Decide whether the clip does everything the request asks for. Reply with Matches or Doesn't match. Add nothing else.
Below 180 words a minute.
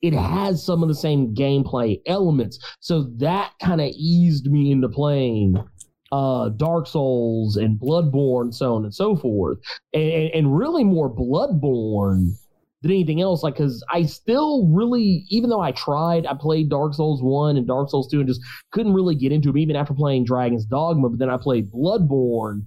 Doesn't match